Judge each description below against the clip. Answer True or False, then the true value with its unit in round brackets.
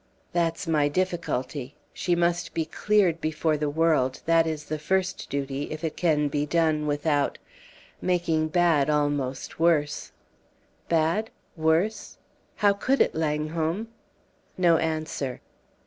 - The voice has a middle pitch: True (160 Hz)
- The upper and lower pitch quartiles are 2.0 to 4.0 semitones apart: True (2.5 semitones)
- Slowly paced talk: True (125 wpm)